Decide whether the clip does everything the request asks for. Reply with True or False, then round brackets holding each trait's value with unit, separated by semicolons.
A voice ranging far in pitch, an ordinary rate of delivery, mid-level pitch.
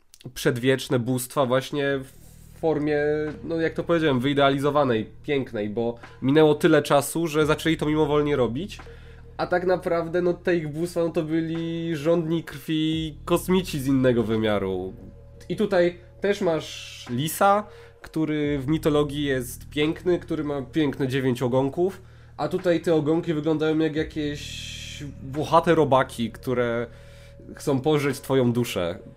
False (4.2 semitones; 130 wpm; 150 Hz)